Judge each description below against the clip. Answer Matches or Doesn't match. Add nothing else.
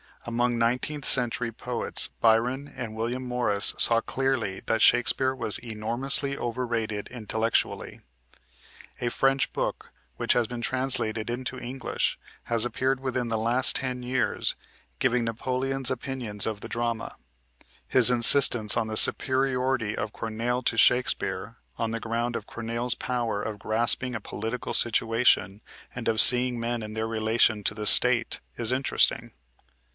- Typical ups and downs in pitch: Doesn't match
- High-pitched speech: Doesn't match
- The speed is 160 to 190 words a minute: Doesn't match